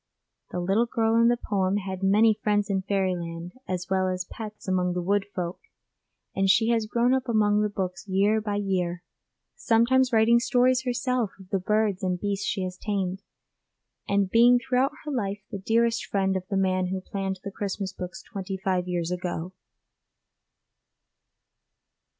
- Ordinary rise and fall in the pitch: Yes, average, 3.1 semitones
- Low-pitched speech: No, high, 200 Hz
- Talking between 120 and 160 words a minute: No, average, 170 wpm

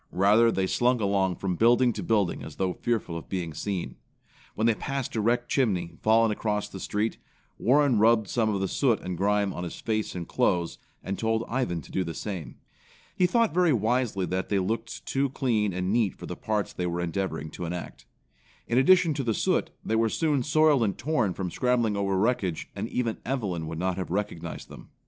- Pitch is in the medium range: No, low, 105 Hz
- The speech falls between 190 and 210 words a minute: Yes, fast, 205 wpm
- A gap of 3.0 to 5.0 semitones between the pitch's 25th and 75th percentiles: Yes, average, 4.6 semitones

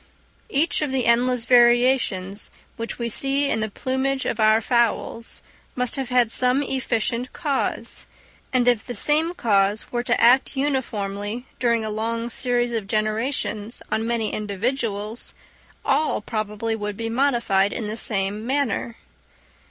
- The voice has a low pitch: No, high, 235 Hz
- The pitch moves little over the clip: No, average, 3.1 semitones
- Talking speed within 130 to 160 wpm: Yes, average, 145 wpm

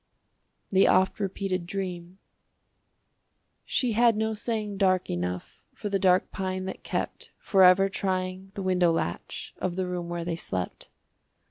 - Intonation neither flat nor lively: No, narrow, 1.6 semitones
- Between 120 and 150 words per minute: Yes, average, 140 wpm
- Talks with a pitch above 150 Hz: Yes, medium, 185 Hz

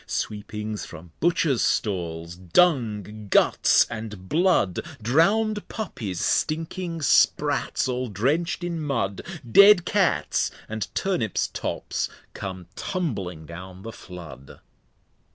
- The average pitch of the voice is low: Yes, low, 110 Hz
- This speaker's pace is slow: Yes, slow, 110 wpm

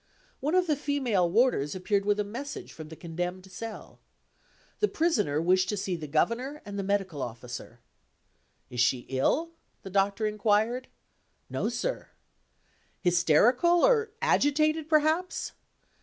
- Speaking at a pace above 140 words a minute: No, slow, 135 wpm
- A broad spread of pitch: Yes, wide, 8.5 semitones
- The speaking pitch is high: Yes, high, 210 Hz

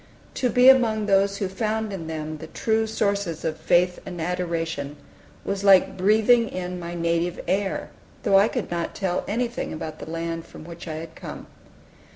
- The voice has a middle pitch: Yes, medium, 180 Hz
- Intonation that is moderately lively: Yes, average, 4.1 semitones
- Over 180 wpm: No, average, 175 wpm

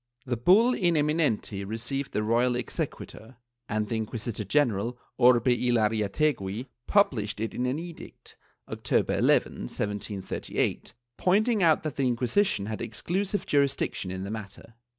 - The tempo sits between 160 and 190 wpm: No, slow, 135 wpm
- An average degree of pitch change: No, wide, 5.9 semitones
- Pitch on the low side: Yes, low, 120 Hz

